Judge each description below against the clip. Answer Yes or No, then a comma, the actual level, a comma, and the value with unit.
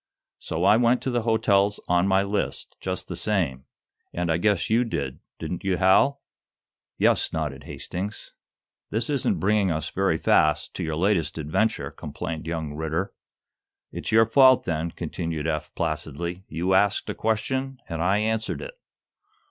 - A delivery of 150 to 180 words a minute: Yes, average, 155 wpm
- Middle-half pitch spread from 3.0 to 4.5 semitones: No, average, 5.2 semitones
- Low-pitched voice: Yes, very low, 95 Hz